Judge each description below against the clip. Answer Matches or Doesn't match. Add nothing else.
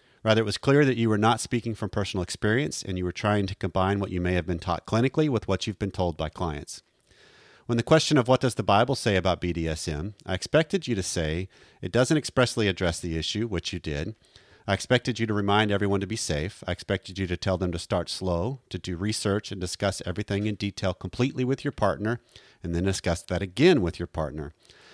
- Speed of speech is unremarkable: Doesn't match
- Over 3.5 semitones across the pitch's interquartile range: Matches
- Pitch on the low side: Matches